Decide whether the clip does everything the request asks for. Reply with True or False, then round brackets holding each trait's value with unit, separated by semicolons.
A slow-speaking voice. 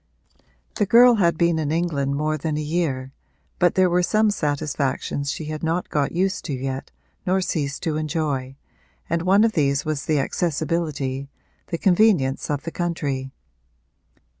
False (160 wpm)